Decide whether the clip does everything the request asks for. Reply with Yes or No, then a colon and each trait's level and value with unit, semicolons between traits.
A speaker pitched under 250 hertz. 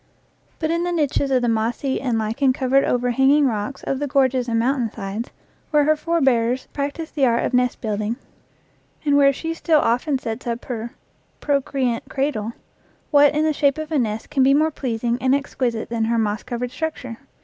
No: very high, 260 Hz